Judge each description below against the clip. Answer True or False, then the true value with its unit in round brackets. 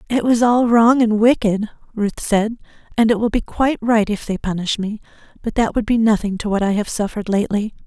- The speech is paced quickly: True (220 wpm)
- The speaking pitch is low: False (220 Hz)